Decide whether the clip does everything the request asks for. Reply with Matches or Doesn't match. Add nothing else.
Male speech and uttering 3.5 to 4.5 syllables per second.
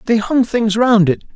Matches